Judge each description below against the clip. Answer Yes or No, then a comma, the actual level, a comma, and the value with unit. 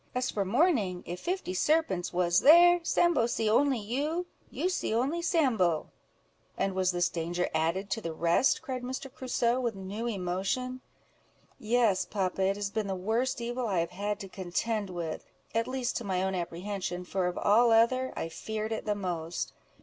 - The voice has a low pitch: No, high, 210 Hz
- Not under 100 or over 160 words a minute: No, average, 175 wpm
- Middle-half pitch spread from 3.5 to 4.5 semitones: No, wide, 5.6 semitones